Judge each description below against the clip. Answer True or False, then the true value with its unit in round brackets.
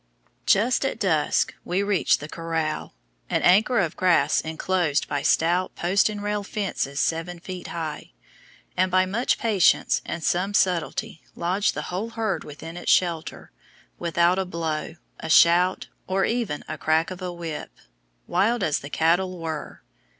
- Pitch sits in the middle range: True (175 Hz)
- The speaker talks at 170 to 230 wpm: False (155 wpm)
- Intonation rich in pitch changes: False (3.0 semitones)